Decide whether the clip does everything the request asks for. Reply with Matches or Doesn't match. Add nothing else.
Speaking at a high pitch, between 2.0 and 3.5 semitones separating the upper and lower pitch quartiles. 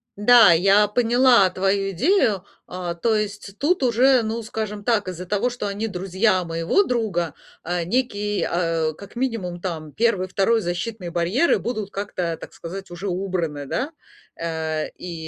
Doesn't match